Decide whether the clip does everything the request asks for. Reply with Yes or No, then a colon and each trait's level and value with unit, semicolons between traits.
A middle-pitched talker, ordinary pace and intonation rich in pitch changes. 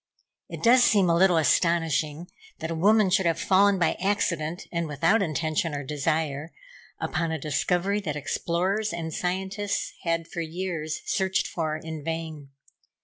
No: medium, 170 Hz; average, 150 wpm; average, 3.2 semitones